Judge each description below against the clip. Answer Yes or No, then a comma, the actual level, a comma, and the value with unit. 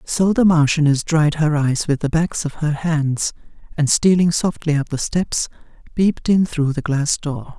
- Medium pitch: Yes, medium, 155 Hz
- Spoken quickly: No, average, 190 wpm